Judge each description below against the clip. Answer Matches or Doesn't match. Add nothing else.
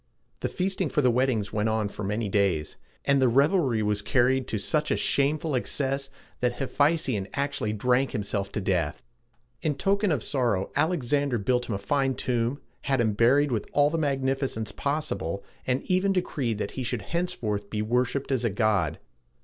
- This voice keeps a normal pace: Matches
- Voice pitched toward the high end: Doesn't match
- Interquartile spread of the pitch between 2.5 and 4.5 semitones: Doesn't match